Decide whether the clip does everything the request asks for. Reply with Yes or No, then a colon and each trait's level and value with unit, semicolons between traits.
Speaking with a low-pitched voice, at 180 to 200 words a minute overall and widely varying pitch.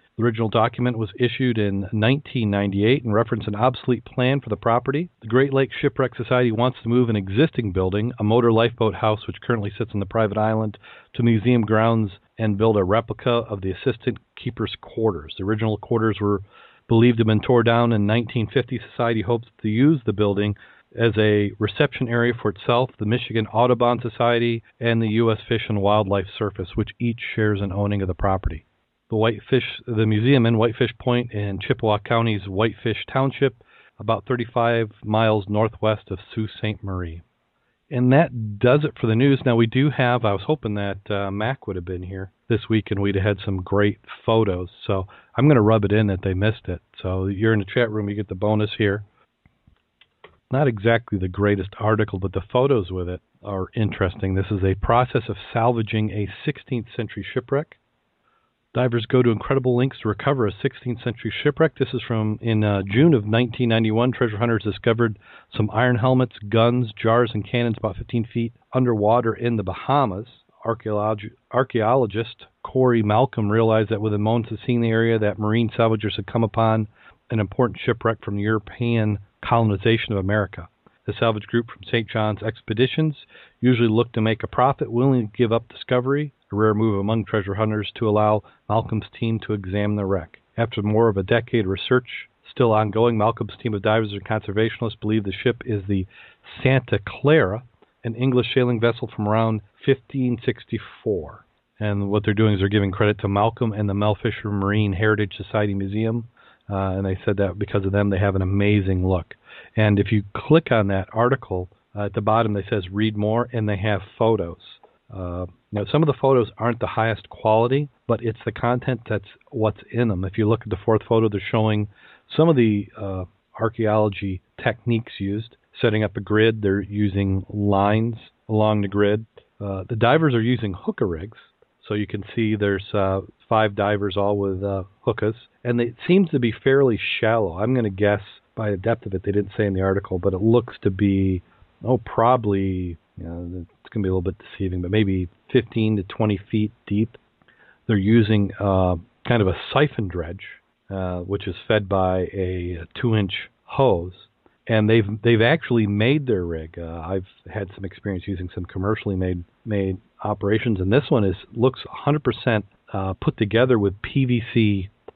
No: low, 110 Hz; average, 185 wpm; average, 2.7 semitones